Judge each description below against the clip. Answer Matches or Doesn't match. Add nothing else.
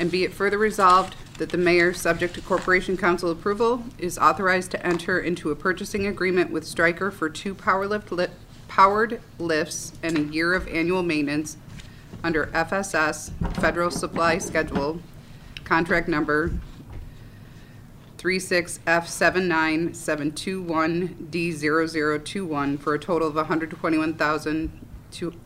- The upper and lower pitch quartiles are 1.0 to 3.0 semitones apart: Matches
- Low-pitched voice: Doesn't match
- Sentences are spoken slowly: Matches